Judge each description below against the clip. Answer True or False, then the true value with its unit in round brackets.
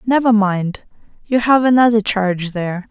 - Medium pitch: False (215 Hz)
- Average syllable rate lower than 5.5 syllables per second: True (5.0 syllables/s)